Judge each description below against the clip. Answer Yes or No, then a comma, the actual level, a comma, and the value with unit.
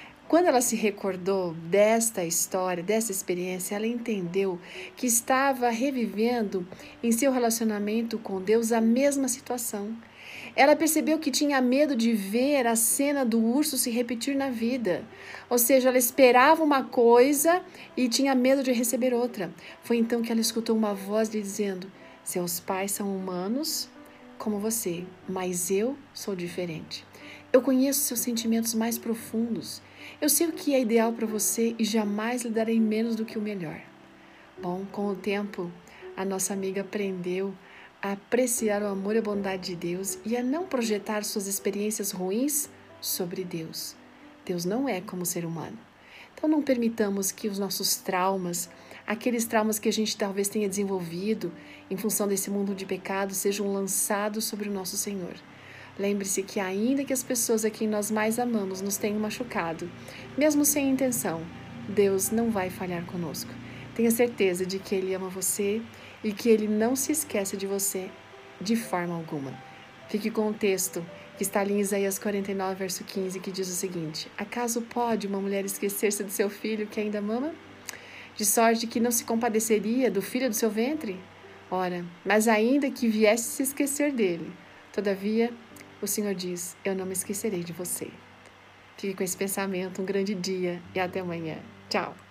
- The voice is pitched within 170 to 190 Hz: No, high, 210 Hz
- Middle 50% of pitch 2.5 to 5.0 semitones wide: Yes, average, 3.6 semitones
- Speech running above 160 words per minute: Yes, average, 170 wpm